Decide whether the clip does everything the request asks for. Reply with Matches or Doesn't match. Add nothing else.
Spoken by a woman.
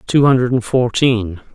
Doesn't match